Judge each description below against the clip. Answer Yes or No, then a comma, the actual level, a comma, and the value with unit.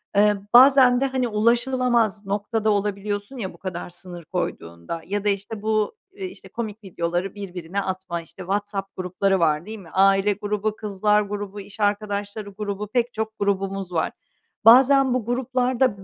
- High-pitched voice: Yes, high, 205 Hz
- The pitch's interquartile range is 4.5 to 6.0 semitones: No, narrow, 2.6 semitones